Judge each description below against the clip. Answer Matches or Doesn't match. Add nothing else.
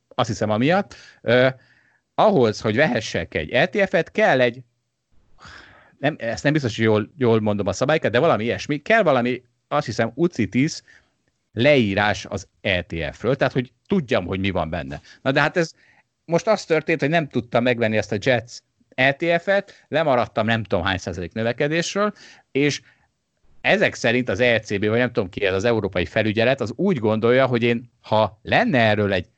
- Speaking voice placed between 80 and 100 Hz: Doesn't match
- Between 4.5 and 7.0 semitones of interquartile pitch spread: Matches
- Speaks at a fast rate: Matches